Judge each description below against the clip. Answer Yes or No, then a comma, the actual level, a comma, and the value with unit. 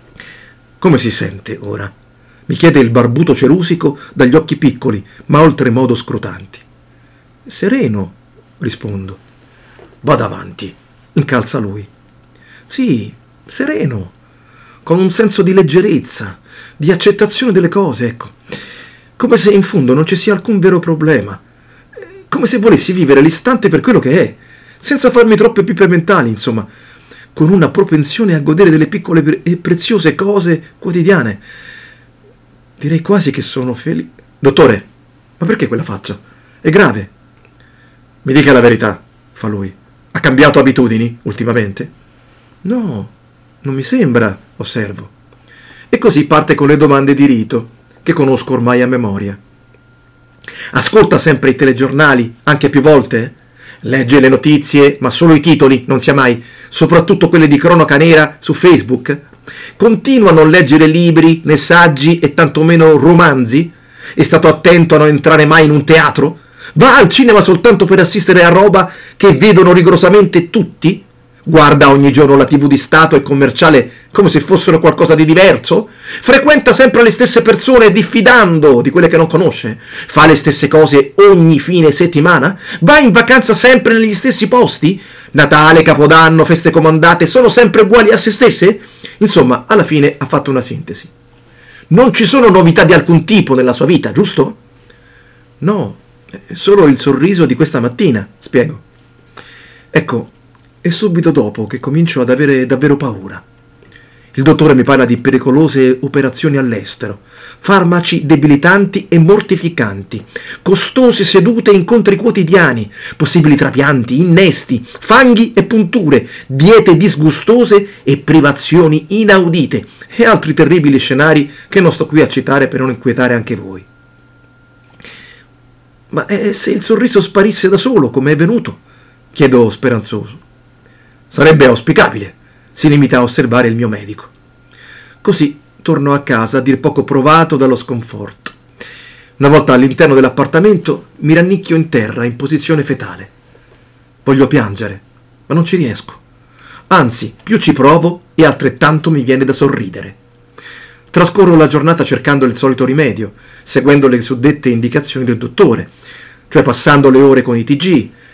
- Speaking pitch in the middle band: Yes, medium, 150 Hz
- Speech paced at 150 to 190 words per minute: No, average, 140 wpm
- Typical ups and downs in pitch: No, wide, 5.9 semitones